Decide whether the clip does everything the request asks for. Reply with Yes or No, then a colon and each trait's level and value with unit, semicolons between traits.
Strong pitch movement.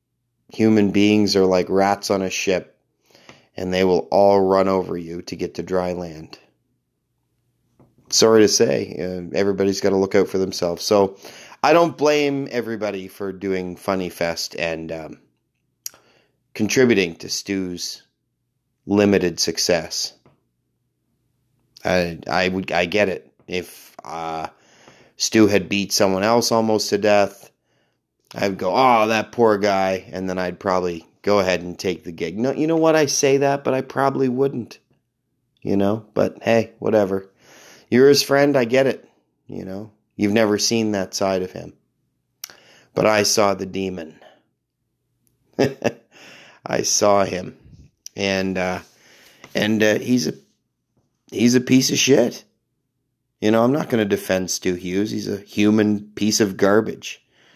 No: average, 3.7 semitones